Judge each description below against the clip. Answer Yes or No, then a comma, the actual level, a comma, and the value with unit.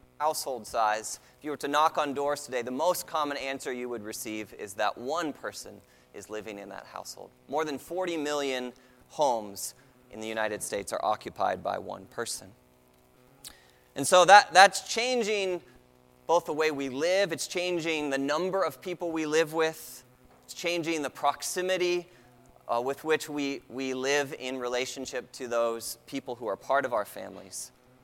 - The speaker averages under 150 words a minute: No, average, 170 wpm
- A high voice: No, low, 135 Hz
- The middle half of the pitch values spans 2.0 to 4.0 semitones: No, average, 5.1 semitones